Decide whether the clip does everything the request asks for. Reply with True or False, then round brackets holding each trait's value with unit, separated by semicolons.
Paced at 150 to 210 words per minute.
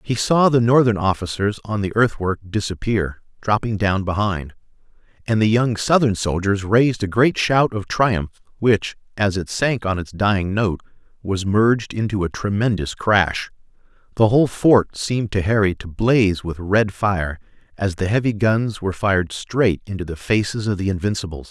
True (170 wpm)